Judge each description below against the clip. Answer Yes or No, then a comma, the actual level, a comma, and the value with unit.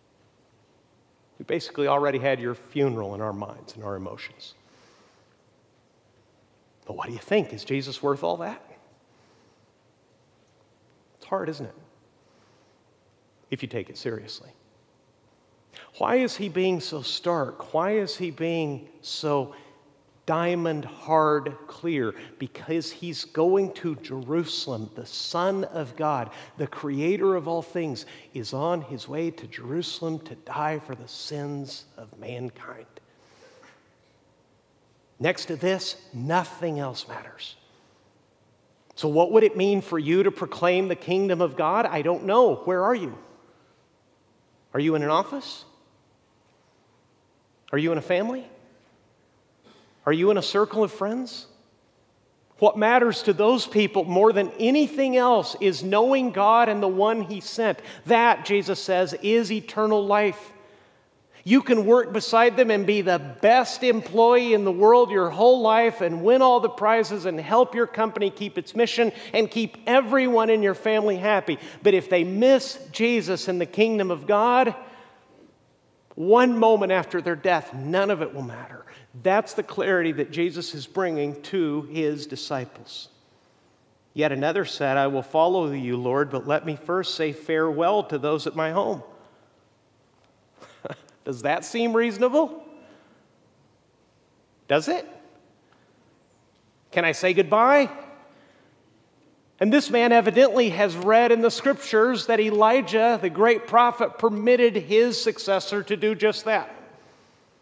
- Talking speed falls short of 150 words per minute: Yes, average, 140 wpm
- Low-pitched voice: No, medium, 185 Hz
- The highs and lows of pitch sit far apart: Yes, wide, 6.4 semitones